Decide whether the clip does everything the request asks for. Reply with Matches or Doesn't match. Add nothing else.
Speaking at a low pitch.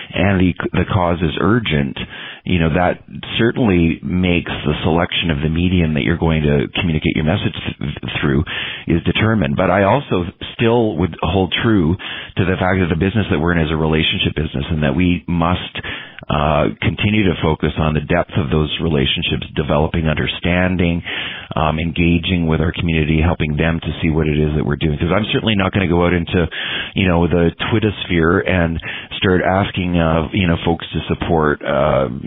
Matches